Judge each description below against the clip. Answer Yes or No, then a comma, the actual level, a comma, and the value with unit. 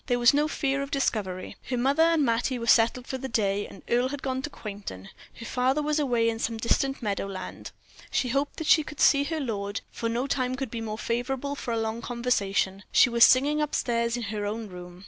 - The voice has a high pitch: Yes, high, 240 Hz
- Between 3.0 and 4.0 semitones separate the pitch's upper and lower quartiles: Yes, average, 3.7 semitones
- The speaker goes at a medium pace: No, fast, 225 wpm